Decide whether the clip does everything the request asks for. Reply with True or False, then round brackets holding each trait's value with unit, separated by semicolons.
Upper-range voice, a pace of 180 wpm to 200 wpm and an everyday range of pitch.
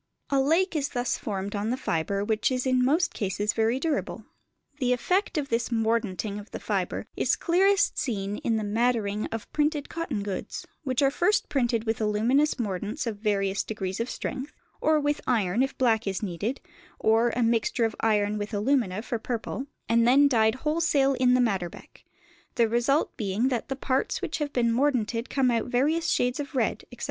True (235 Hz; 190 wpm; 4.3 semitones)